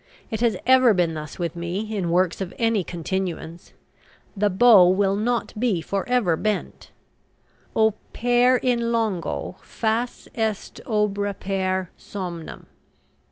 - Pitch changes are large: No, average, 4.0 semitones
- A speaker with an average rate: No, slow, 120 wpm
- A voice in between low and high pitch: No, high, 200 Hz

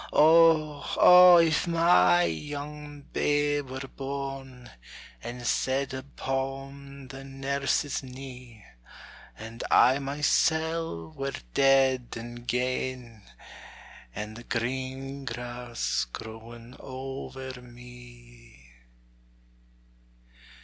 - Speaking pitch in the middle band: No, low, 130 Hz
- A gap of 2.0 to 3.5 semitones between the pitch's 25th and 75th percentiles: Yes, narrow, 2.5 semitones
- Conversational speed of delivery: No, slow, 80 wpm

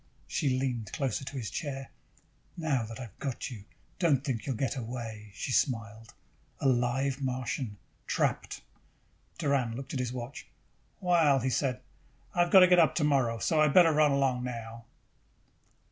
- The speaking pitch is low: Yes, low, 130 Hz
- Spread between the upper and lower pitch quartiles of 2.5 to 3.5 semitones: Yes, average, 3.2 semitones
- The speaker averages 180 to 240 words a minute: No, average, 165 wpm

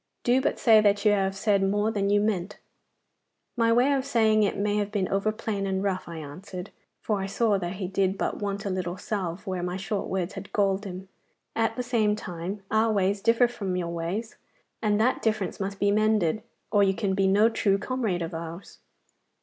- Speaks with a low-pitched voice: No, high, 200 Hz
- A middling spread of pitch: No, narrow, 2.2 semitones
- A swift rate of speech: Yes, fast, 210 wpm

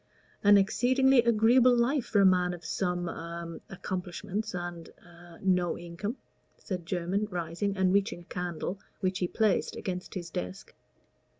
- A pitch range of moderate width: Yes, average, 3.1 semitones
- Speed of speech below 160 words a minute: Yes, average, 145 wpm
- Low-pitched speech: No, medium, 185 Hz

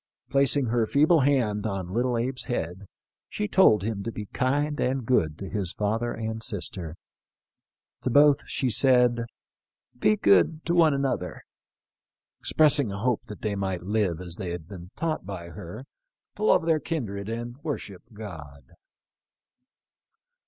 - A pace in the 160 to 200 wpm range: No, average, 150 wpm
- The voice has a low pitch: Yes, low, 115 Hz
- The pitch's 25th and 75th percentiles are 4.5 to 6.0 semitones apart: Yes, wide, 5.5 semitones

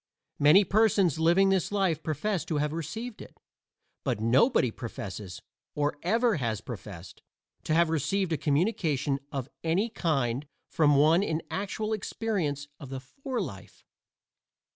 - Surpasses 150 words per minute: No, average, 140 wpm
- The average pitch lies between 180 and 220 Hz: No, medium, 160 Hz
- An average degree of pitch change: No, wide, 6.1 semitones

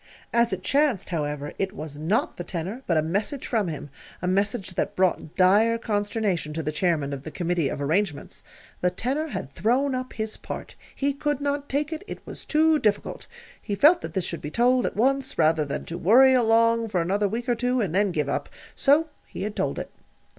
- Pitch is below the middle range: No, high, 205 Hz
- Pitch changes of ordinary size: No, wide, 6.9 semitones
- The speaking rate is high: Yes, fast, 210 wpm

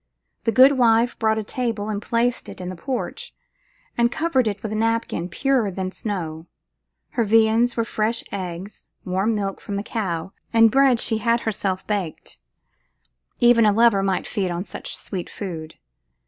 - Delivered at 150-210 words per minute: Yes, average, 170 wpm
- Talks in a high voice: Yes, high, 220 Hz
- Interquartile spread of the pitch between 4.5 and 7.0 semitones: No, average, 3.5 semitones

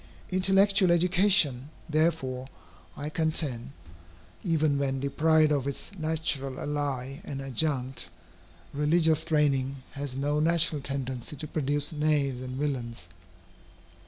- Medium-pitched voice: Yes, medium, 145 Hz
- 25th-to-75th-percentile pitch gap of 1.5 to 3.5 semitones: Yes, average, 2.8 semitones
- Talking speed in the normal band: No, slow, 105 wpm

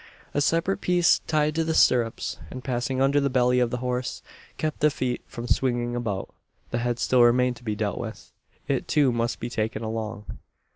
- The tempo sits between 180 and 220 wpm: Yes, average, 195 wpm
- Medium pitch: No, low, 125 Hz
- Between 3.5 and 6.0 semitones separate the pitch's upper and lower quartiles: No, average, 2.8 semitones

